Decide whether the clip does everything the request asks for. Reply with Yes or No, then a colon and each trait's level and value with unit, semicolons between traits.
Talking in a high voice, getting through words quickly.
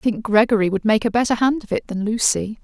Yes: high, 220 Hz; fast, 275 wpm